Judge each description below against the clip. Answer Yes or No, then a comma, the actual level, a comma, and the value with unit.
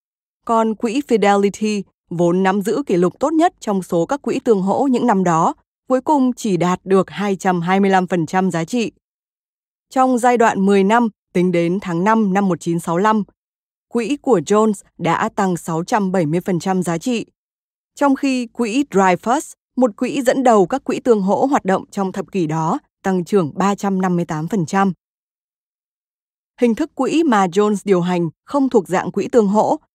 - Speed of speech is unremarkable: No, slow, 160 wpm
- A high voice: Yes, high, 200 Hz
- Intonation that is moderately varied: Yes, average, 4.6 semitones